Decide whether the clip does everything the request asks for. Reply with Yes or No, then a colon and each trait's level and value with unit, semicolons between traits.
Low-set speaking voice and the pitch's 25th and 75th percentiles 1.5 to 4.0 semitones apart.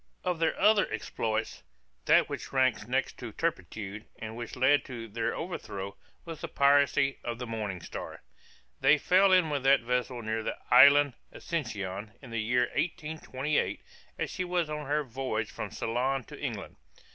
No: low, 130 Hz; average, 5.0 semitones